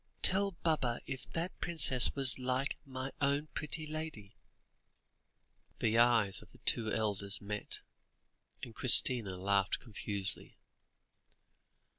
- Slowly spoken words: Yes, slow, 110 wpm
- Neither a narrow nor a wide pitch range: No, wide, 5.8 semitones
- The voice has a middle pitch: No, low, 125 Hz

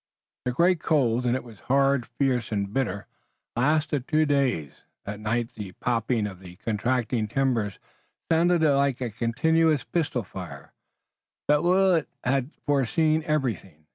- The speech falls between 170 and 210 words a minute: No, average, 140 wpm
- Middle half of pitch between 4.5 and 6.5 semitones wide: Yes, average, 5.1 semitones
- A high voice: No, low, 130 Hz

